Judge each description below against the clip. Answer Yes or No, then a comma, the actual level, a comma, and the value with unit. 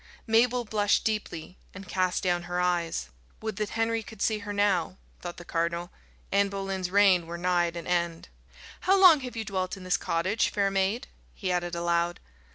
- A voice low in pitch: No, medium, 185 Hz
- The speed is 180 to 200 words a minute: Yes, average, 185 wpm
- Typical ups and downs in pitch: Yes, average, 3.3 semitones